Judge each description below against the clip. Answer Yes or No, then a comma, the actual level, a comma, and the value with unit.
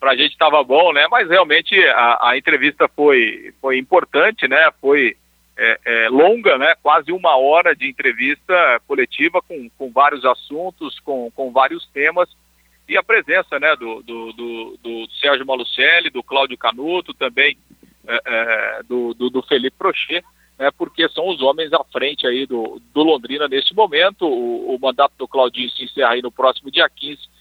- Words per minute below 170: No, average, 175 wpm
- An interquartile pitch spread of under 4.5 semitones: No, wide, 5.5 semitones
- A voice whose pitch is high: No, low, 135 Hz